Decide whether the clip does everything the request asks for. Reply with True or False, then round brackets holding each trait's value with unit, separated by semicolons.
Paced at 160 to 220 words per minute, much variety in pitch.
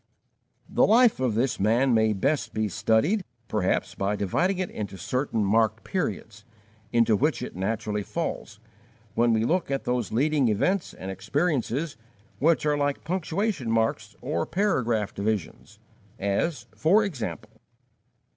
False (140 wpm; 6.3 semitones)